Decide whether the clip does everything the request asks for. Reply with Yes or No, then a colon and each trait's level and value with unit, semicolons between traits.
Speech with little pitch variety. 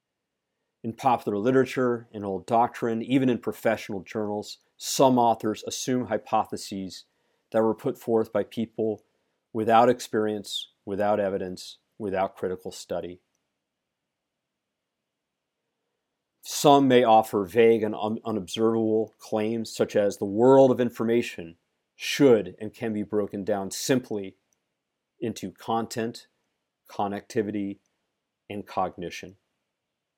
Yes: narrow, 2.3 semitones